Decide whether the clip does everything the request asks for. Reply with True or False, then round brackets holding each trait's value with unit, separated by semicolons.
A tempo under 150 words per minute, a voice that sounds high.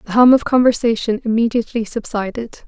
True (135 wpm; 230 Hz)